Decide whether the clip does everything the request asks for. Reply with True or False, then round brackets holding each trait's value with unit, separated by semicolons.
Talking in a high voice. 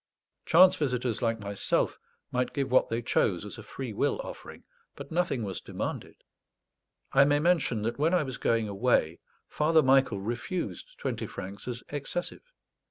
False (125 Hz)